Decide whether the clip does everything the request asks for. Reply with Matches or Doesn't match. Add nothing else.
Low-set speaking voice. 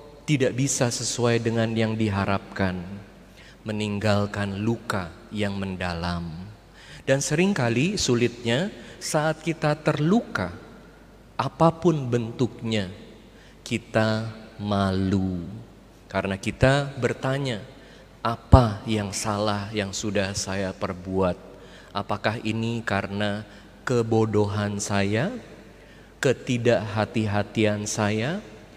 Matches